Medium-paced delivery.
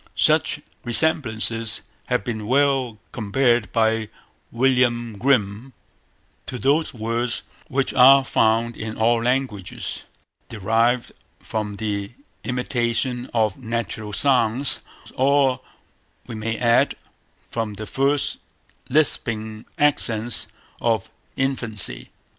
No: slow, 95 wpm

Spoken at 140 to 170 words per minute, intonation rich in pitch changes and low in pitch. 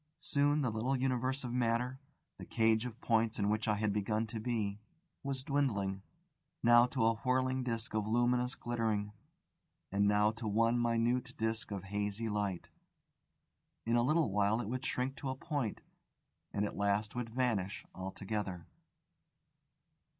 No: average, 155 wpm; average, 3.2 semitones; low, 115 Hz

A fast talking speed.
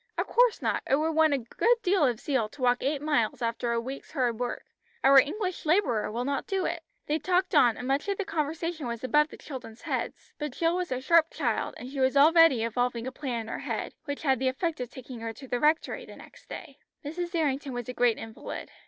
Yes: fast, 240 wpm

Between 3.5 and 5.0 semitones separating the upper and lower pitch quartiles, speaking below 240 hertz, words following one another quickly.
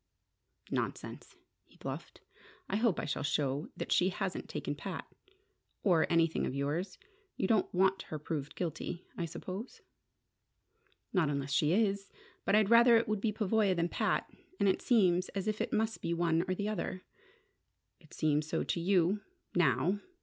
No: average, 4.1 semitones; medium, 185 Hz; average, 165 wpm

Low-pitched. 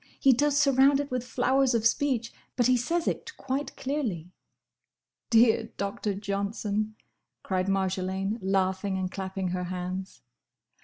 No: high, 215 Hz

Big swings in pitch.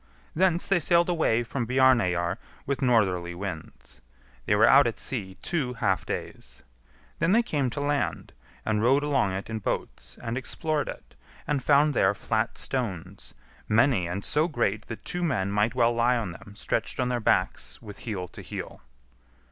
Yes: wide, 5.9 semitones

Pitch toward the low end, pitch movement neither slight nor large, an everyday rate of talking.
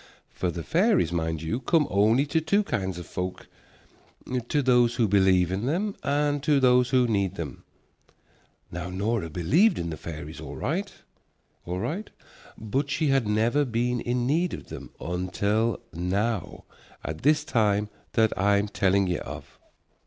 No: low, 110 Hz; wide, 7.3 semitones; average, 160 wpm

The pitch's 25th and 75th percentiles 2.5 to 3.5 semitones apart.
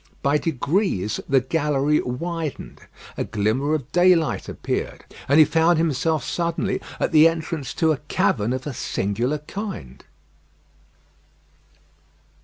No: average, 4.2 semitones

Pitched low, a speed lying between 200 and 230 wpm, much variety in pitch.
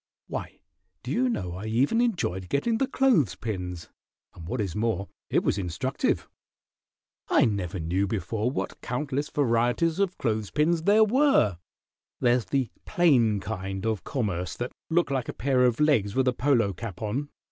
No: low, 120 Hz; average, 165 wpm; wide, 6.9 semitones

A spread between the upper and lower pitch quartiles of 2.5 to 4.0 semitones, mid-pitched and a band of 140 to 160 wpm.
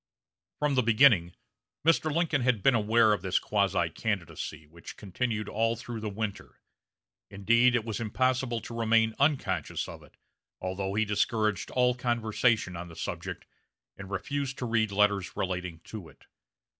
No: average, 3.7 semitones; low, 110 Hz; average, 155 wpm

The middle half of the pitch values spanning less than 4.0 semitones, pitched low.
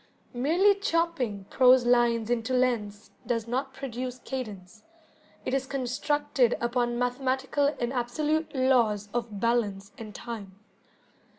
No: narrow, 2.6 semitones; high, 245 Hz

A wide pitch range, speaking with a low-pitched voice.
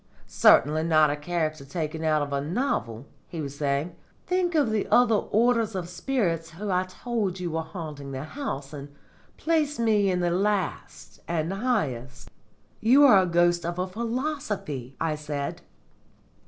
No: wide, 6.4 semitones; medium, 175 Hz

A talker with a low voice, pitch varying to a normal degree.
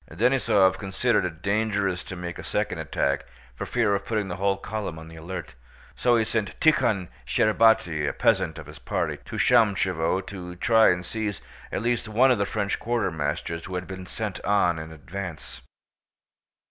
Yes: very low, 95 Hz; average, 4.0 semitones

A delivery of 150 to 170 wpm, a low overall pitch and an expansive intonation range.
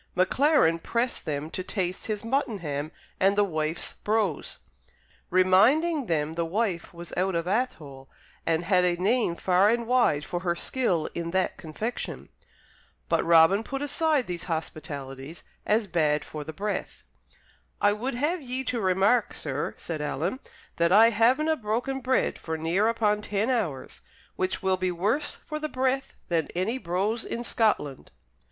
No: average, 155 wpm; high, 190 Hz; wide, 6.0 semitones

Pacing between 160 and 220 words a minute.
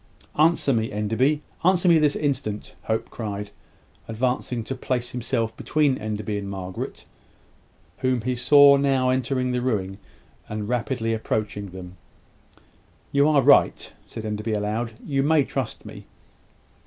No: slow, 135 wpm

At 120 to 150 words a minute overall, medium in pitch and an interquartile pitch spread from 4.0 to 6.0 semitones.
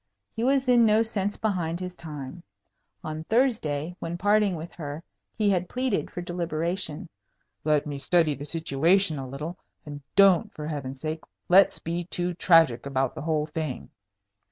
No: average, 160 wpm; medium, 165 Hz; average, 4.4 semitones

